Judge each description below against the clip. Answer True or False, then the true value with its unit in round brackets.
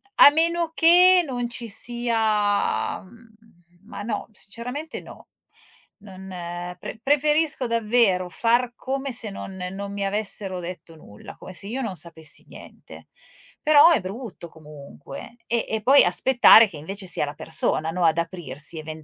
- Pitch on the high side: True (215 Hz)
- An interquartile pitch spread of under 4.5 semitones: False (5.5 semitones)